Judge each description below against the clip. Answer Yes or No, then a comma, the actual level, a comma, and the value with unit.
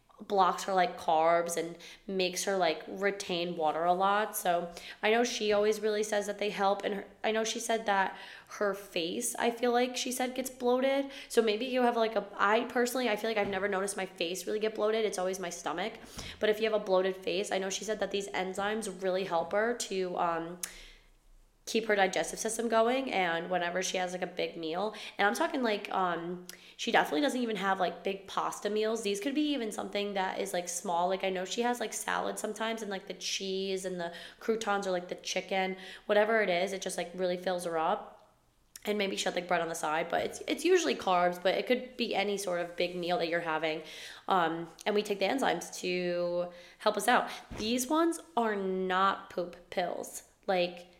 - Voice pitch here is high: Yes, high, 195 Hz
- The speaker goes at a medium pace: No, fast, 220 wpm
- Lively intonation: No, average, 3.5 semitones